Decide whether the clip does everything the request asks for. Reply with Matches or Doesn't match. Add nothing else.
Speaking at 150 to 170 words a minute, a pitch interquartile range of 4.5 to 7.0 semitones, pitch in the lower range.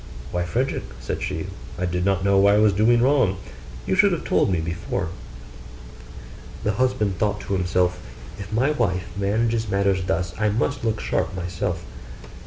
Doesn't match